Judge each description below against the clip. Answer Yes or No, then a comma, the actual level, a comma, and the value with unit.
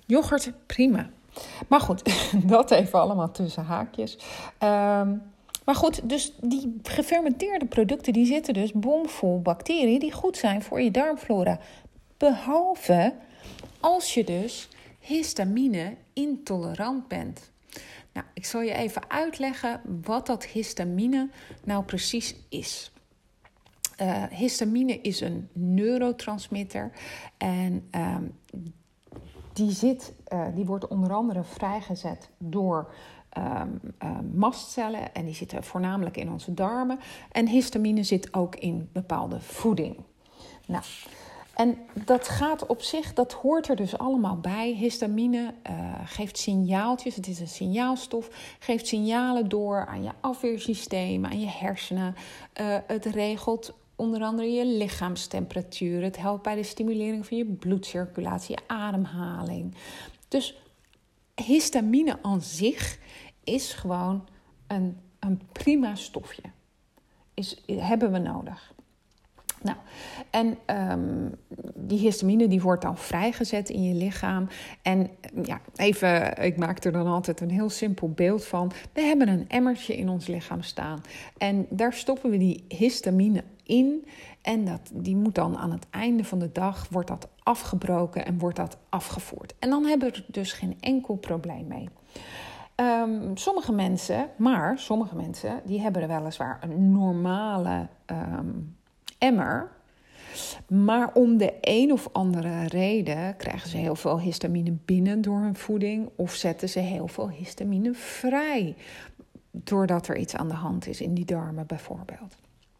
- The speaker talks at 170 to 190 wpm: No, slow, 135 wpm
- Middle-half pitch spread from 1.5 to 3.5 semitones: No, average, 4.7 semitones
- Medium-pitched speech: No, high, 205 Hz